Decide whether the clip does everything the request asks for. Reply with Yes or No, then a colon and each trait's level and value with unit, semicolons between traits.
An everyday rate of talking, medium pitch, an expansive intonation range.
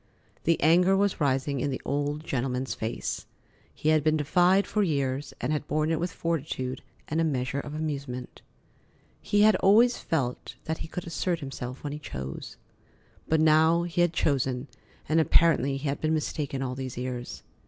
No: average, 175 wpm; medium, 150 Hz; average, 3.5 semitones